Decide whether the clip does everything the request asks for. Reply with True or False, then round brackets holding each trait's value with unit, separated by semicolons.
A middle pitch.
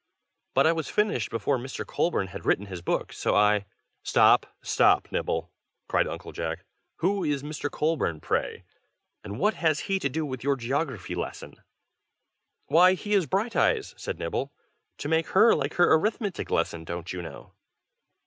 True (145 Hz)